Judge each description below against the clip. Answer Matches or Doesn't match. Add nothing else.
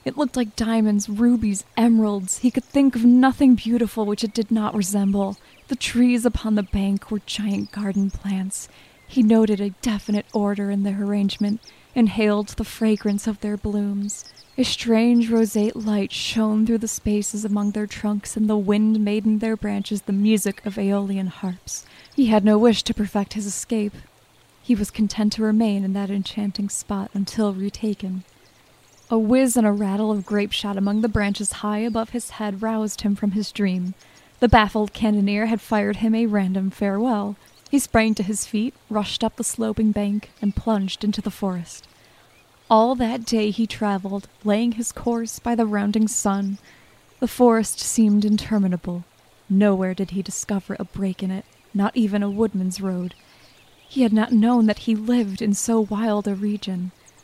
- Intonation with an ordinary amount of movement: Doesn't match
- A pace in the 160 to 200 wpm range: Matches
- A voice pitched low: Doesn't match